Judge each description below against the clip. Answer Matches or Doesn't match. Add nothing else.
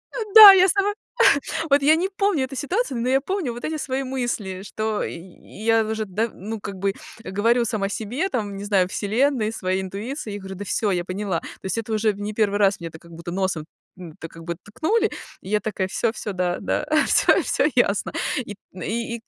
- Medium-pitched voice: Doesn't match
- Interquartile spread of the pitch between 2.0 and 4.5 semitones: Doesn't match